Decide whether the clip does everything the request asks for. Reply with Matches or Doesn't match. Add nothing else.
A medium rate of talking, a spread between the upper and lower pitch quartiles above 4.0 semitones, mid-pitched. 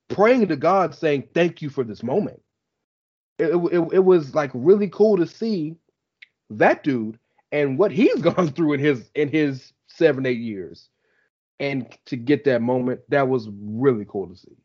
Matches